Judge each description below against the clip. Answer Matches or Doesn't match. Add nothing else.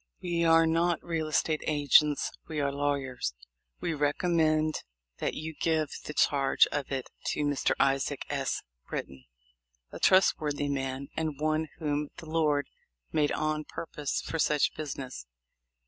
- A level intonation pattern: Matches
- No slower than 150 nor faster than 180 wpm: Doesn't match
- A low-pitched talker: Doesn't match